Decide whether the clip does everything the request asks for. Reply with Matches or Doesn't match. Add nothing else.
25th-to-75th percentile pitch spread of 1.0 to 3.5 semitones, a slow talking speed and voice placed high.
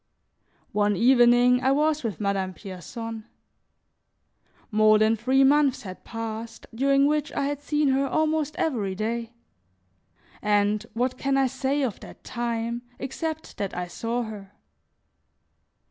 Doesn't match